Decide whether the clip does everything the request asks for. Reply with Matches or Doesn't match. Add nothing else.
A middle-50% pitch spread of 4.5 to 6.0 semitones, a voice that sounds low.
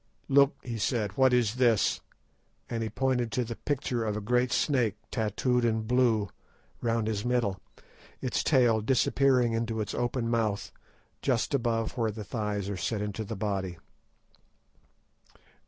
Doesn't match